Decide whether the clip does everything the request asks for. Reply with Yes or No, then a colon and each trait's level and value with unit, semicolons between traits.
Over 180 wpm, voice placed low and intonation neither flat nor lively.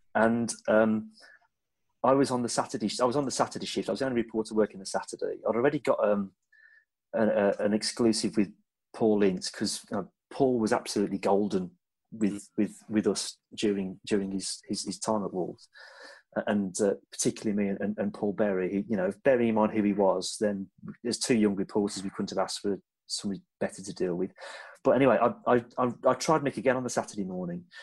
Yes: average, 200 wpm; low, 110 Hz; average, 3.5 semitones